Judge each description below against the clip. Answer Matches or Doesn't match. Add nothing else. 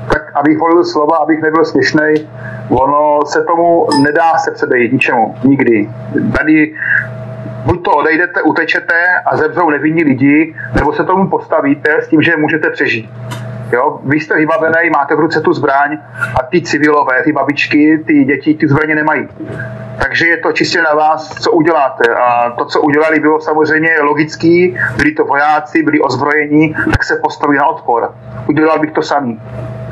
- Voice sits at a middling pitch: Matches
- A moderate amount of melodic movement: Doesn't match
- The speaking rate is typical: Matches